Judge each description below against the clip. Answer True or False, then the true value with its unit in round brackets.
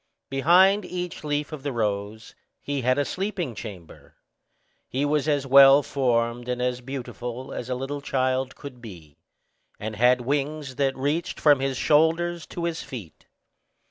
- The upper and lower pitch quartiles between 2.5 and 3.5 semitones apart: True (3.2 semitones)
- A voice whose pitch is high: False (135 Hz)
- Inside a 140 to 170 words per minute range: True (155 wpm)